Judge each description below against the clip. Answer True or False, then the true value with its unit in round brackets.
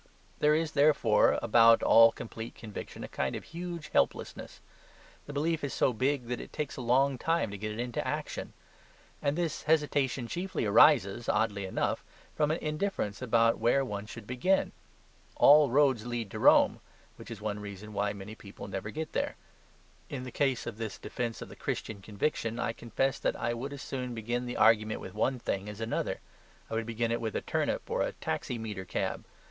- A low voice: True (120 Hz)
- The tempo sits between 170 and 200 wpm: True (190 wpm)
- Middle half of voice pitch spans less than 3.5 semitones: False (4.6 semitones)